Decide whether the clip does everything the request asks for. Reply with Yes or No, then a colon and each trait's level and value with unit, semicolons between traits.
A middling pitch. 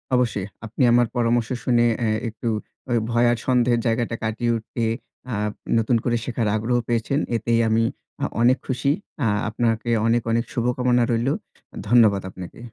No: low, 120 Hz